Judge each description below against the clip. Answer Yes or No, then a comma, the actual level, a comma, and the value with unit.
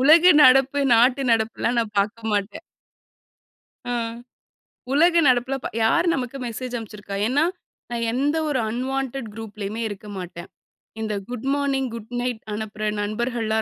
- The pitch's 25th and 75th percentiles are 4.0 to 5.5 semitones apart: No, average, 3.6 semitones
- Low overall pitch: No, high, 235 Hz